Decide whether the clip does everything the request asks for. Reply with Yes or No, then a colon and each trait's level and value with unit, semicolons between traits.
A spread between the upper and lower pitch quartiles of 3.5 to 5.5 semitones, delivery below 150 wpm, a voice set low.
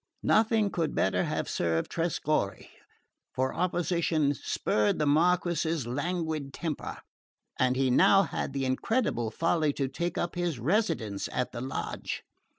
No: average, 5.1 semitones; slow, 135 wpm; medium, 155 Hz